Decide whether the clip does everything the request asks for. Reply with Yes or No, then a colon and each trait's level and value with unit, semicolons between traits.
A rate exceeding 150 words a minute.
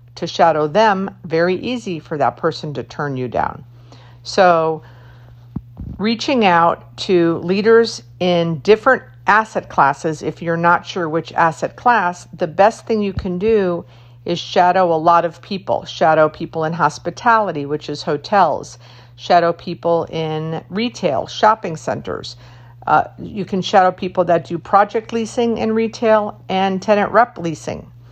No: average, 145 wpm